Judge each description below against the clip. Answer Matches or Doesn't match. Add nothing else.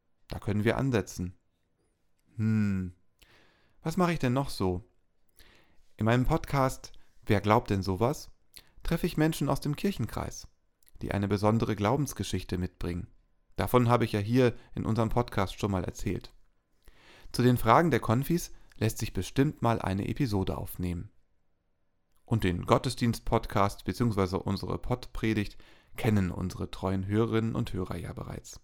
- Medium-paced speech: Matches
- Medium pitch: Doesn't match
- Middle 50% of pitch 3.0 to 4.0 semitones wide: Doesn't match